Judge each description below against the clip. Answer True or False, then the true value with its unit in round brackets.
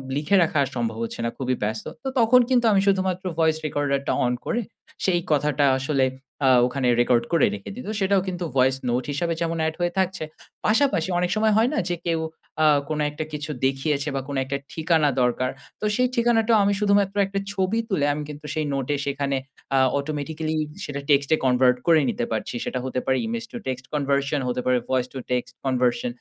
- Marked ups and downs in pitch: True (6.1 semitones)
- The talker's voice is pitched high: False (150 Hz)